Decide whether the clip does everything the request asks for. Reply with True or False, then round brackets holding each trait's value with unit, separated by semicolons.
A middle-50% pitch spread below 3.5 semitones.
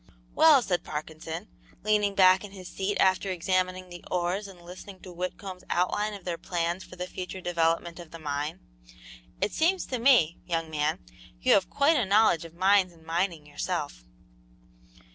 True (2.9 semitones)